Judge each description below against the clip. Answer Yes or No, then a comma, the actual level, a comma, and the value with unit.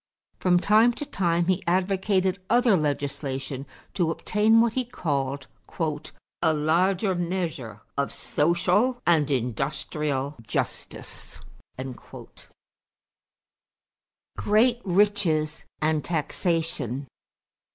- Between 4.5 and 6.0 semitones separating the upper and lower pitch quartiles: Yes, average, 5.1 semitones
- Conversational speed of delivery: No, slow, 85 wpm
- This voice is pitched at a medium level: Yes, medium, 170 Hz